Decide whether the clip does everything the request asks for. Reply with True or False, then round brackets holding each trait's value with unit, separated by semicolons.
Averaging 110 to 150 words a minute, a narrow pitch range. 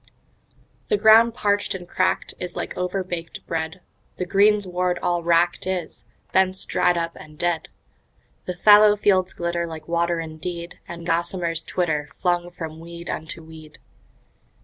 True (140 wpm; 1.9 semitones)